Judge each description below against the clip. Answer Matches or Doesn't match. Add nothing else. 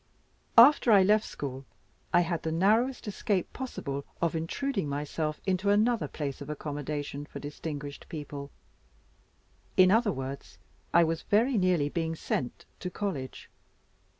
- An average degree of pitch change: Doesn't match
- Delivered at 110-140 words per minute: Matches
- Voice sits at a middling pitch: Matches